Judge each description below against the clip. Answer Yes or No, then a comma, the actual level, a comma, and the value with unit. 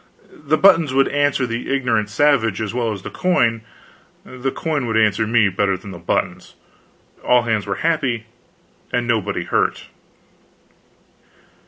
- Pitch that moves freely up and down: No, average, 4.3 semitones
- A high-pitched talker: No, low, 120 Hz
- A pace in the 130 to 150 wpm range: Yes, average, 145 wpm